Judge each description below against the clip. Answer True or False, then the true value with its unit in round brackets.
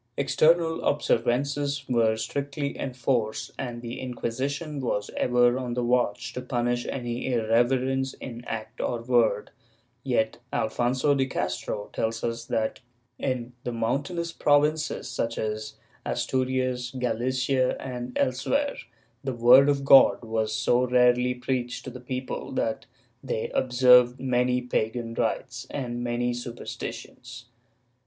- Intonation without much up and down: True (1.8 semitones)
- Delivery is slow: True (125 wpm)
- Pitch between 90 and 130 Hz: True (125 Hz)